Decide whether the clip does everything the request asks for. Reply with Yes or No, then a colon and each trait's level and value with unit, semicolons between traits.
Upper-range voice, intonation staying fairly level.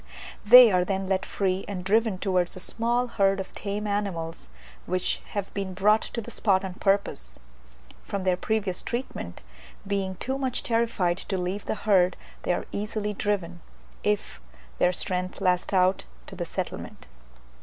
Yes: high, 195 Hz; narrow, 2.3 semitones